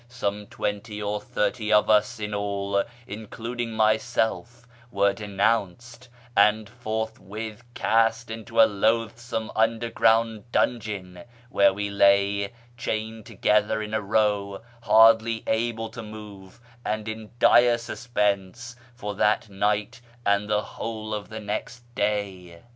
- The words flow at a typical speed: No, slow, 125 wpm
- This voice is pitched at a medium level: No, low, 110 Hz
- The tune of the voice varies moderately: No, narrow, 1.8 semitones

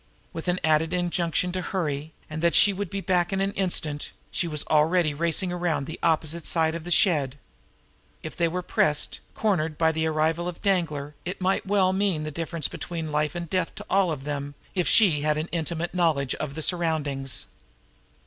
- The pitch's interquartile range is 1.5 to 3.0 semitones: Yes, average, 2.7 semitones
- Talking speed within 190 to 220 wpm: Yes, average, 195 wpm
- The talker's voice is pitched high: No, medium, 165 Hz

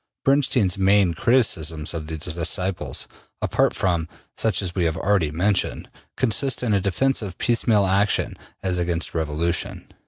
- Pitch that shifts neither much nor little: Yes, average, 4.0 semitones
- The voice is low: Yes, very low, 95 Hz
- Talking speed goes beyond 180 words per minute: No, average, 145 wpm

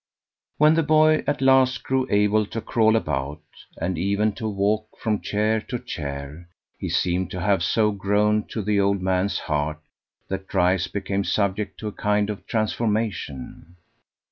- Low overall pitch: Yes, low, 105 Hz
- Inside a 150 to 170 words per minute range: Yes, average, 160 wpm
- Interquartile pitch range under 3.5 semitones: Yes, average, 2.9 semitones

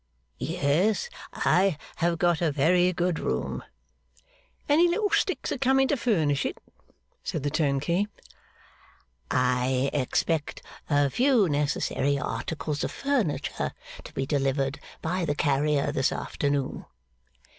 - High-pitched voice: No, medium, 155 Hz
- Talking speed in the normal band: No, slow, 120 wpm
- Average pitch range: Yes, average, 4.7 semitones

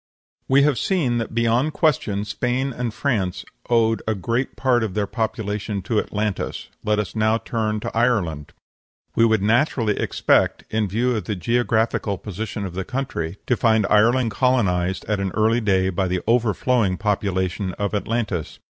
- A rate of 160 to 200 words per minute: Yes, average, 165 wpm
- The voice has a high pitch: No, low, 110 Hz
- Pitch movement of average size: Yes, average, 3.2 semitones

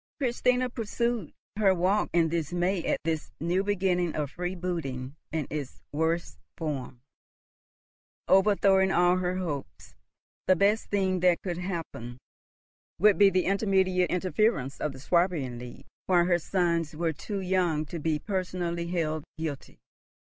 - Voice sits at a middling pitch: Yes, medium, 175 Hz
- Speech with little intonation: No, average, 3.1 semitones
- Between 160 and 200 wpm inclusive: No, slow, 135 wpm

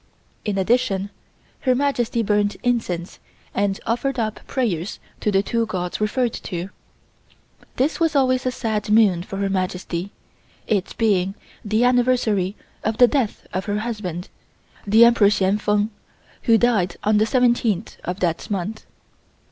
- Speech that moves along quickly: No, average, 145 wpm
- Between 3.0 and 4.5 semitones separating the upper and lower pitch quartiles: Yes, average, 3.7 semitones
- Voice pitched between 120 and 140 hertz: No, high, 210 Hz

